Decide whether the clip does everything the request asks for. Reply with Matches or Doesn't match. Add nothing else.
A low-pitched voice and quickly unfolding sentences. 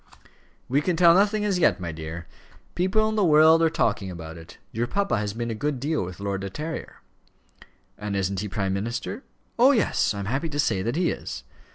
Matches